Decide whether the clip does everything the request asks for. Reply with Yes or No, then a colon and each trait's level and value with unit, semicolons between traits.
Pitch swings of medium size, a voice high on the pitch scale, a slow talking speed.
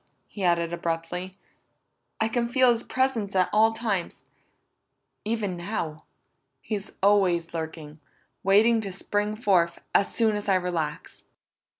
Yes: average, 4.3 semitones; high, 195 Hz; slow, 125 wpm